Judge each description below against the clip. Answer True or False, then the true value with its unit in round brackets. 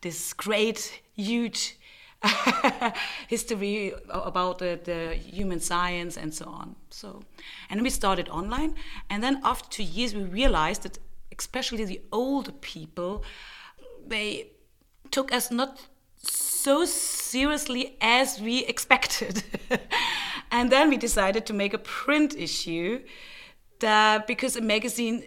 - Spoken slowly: True (125 wpm)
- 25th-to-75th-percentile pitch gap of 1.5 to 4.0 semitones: False (4.9 semitones)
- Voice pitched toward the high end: True (230 Hz)